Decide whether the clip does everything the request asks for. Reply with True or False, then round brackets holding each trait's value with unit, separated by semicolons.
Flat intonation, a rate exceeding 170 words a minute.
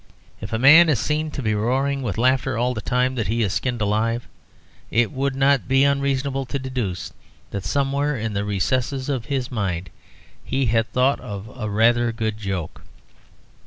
False (3.9 semitones; 180 wpm)